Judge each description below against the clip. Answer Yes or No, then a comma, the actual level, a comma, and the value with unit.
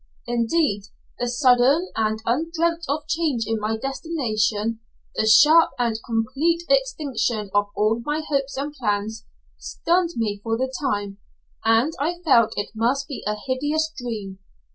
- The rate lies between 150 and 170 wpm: No, average, 140 wpm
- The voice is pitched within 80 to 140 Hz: No, high, 245 Hz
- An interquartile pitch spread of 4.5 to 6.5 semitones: Yes, wide, 5.6 semitones